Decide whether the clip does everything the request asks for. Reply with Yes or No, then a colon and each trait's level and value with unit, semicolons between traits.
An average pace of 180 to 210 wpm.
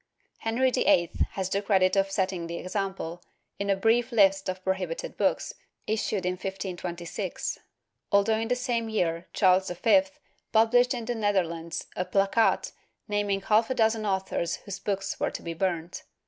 No: average, 160 wpm